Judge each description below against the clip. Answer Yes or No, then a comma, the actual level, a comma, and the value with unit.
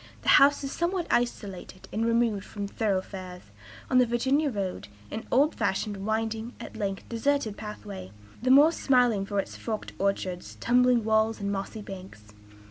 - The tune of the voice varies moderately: Yes, average, 4.0 semitones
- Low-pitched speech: No, high, 220 Hz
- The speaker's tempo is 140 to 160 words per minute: Yes, average, 155 wpm